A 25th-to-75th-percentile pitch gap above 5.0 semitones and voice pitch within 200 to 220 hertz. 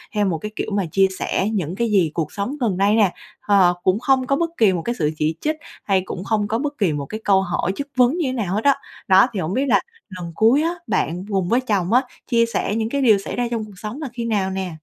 No: average, 4.3 semitones; high, 210 Hz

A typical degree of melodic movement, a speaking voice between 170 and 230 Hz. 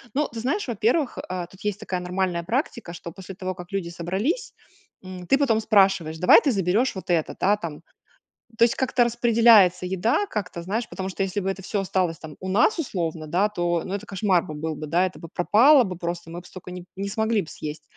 Yes: average, 4.0 semitones; high, 190 Hz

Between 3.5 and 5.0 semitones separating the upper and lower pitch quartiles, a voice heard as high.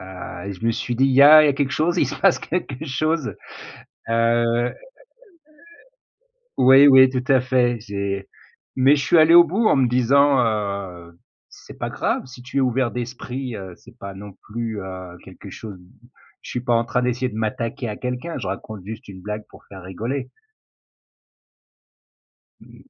No: average, 4.2 semitones; low, 120 Hz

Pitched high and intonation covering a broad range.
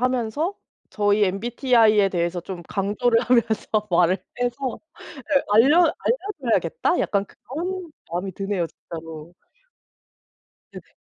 No: high, 215 Hz; average, 5.0 semitones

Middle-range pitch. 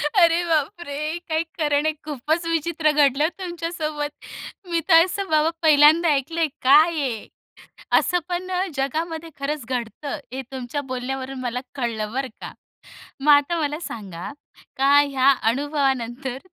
No: very high, 295 Hz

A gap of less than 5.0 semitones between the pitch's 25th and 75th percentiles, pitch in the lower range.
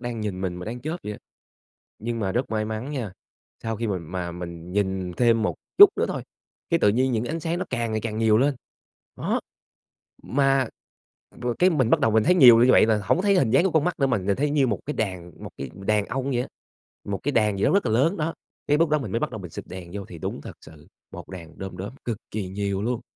No: wide, 5.5 semitones; low, 110 Hz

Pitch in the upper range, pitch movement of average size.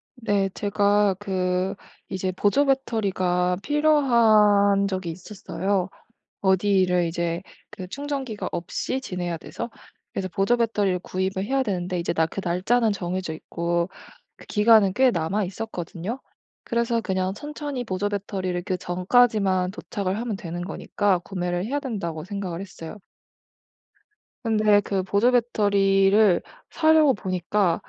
Yes: high, 195 Hz; average, 3.4 semitones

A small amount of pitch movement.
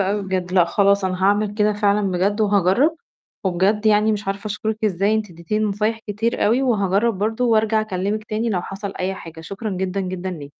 Yes: narrow, 2.3 semitones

